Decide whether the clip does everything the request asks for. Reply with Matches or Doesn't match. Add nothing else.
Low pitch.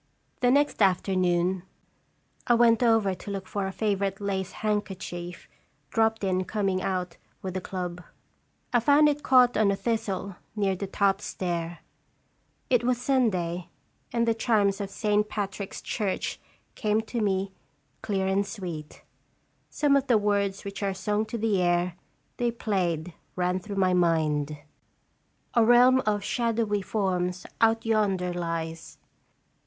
Doesn't match